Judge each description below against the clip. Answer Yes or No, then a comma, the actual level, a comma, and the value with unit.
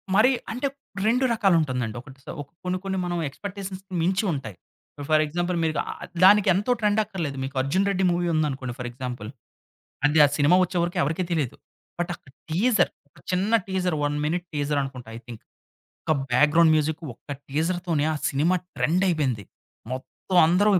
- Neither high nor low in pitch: Yes, medium, 165 Hz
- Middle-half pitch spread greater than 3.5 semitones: Yes, average, 4.8 semitones